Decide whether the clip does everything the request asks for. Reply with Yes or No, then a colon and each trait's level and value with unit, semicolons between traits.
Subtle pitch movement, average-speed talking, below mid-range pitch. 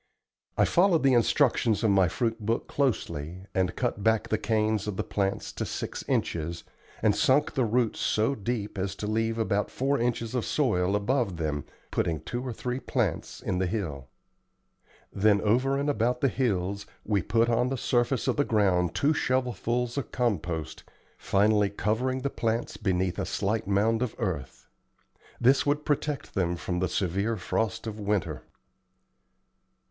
No: average, 4.2 semitones; average, 165 wpm; low, 110 Hz